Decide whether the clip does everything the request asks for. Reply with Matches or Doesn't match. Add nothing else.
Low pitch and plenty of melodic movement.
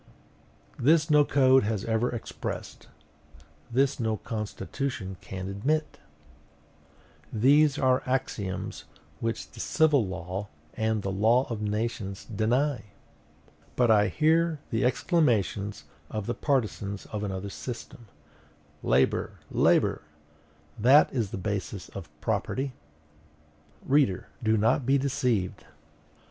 Doesn't match